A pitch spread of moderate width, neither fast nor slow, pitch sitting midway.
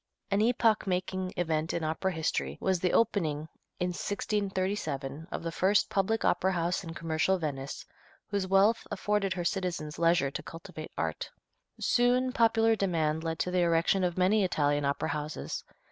Yes: average, 3.7 semitones; average, 160 wpm; medium, 180 Hz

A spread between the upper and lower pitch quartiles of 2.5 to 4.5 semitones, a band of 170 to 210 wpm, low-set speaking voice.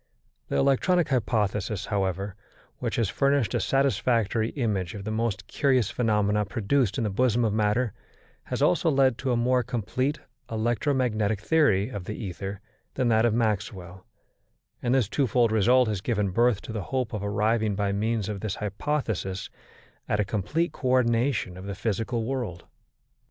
No: average, 3.7 semitones; average, 160 wpm; low, 110 Hz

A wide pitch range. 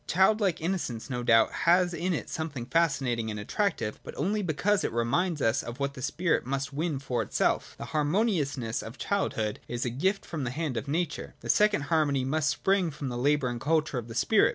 Yes: wide, 6.0 semitones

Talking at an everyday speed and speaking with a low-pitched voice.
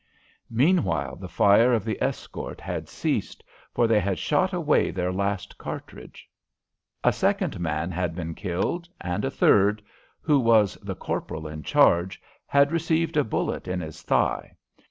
Yes: average, 155 wpm; low, 100 Hz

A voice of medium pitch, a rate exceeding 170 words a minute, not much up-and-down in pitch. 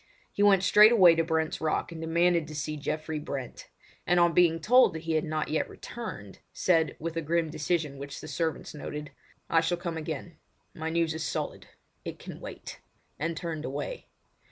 Yes: medium, 160 Hz; average, 180 wpm; narrow, 1.7 semitones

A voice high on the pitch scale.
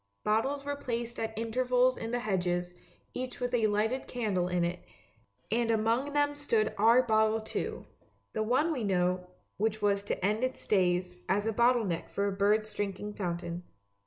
Yes: high, 220 Hz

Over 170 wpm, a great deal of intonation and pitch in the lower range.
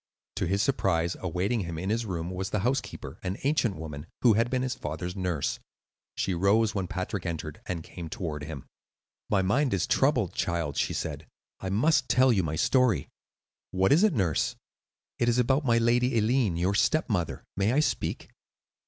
Yes: average, 180 wpm; wide, 5.9 semitones; very low, 95 Hz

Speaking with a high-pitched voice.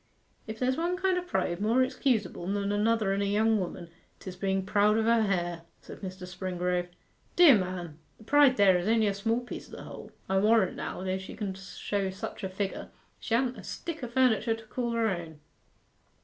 Yes: high, 205 Hz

